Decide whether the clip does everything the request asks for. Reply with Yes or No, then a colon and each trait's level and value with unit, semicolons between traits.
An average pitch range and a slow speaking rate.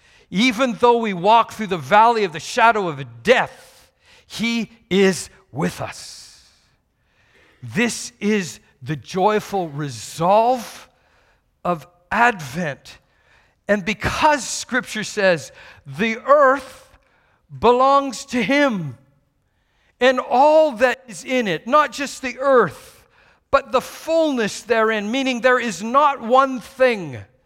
No: wide, 6.1 semitones; slow, 115 wpm